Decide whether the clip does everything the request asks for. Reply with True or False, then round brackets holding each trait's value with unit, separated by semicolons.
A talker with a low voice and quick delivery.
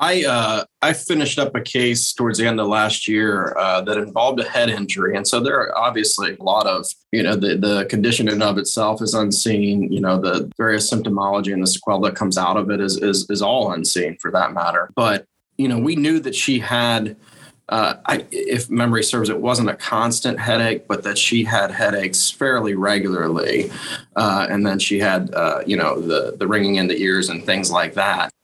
True (105 Hz; 215 wpm)